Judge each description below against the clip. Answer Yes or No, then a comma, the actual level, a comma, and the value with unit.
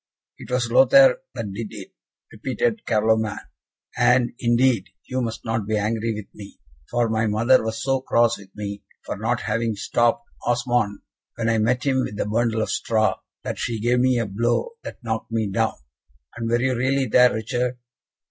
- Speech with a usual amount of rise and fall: No, narrow, 2.2 semitones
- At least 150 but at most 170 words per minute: No, average, 180 wpm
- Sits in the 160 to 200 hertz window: No, low, 115 Hz